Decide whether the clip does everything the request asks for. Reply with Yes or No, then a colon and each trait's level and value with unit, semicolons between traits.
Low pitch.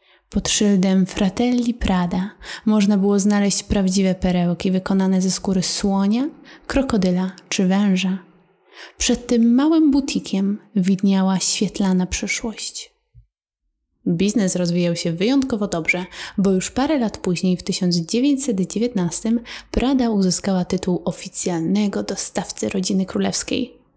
No: high, 195 Hz